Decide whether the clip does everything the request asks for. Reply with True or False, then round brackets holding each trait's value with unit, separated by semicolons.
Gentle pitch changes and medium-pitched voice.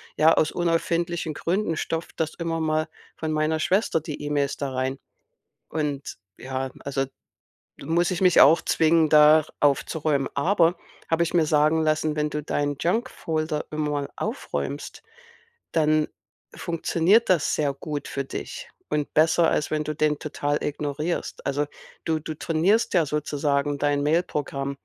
True (2.1 semitones; 155 Hz)